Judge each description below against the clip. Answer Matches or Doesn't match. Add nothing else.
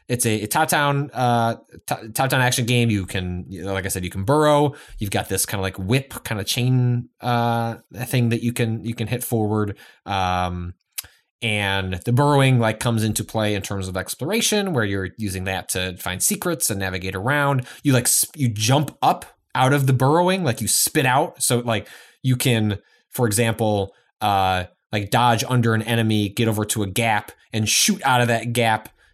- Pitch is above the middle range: Doesn't match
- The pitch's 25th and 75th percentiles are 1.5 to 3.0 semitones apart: Doesn't match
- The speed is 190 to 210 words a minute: Matches